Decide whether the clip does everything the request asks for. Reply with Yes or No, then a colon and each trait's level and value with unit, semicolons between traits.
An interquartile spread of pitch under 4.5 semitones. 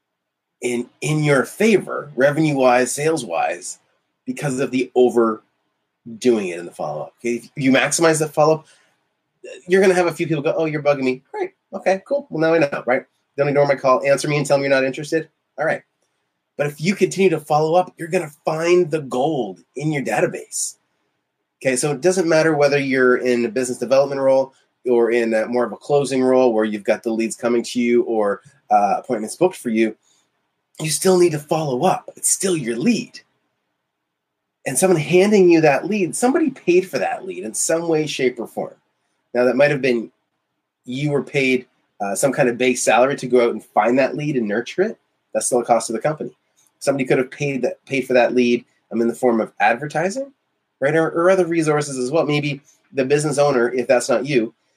No: average, 4.8 semitones